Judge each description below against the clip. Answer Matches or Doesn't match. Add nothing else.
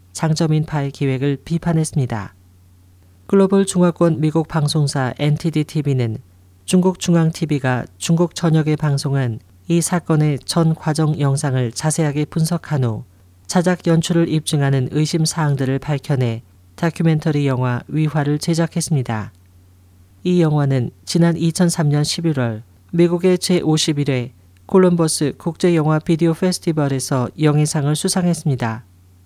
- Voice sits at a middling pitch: Matches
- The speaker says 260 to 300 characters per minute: Matches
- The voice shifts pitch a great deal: Doesn't match